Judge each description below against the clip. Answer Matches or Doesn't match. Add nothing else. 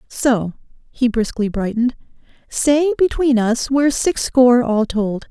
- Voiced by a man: Doesn't match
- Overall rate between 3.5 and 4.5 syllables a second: Matches